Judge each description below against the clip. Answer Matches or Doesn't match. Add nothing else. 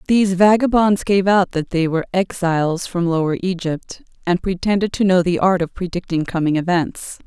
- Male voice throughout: Doesn't match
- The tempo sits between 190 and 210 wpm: Doesn't match